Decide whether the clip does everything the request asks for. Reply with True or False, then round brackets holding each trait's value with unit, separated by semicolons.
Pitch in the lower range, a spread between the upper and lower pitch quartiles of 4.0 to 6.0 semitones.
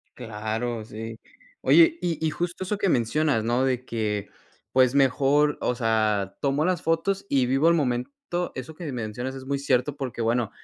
True (130 Hz; 4.7 semitones)